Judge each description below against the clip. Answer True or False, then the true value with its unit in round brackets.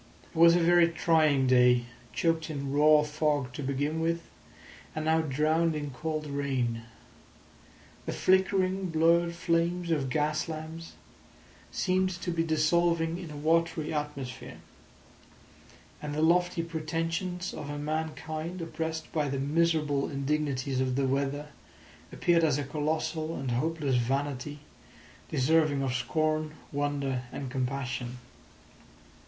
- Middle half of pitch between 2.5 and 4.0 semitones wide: True (2.9 semitones)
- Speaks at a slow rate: True (125 wpm)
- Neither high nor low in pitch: True (155 Hz)